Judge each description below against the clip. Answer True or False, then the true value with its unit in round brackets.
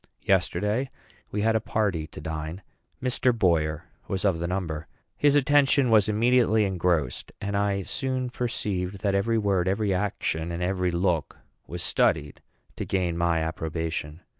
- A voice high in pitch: False (95 Hz)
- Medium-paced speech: True (150 wpm)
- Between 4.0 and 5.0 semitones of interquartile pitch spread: True (4.4 semitones)